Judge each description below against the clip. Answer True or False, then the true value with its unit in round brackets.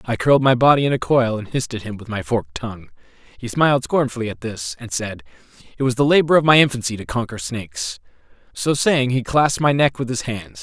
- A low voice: True (125 Hz)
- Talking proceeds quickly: True (230 wpm)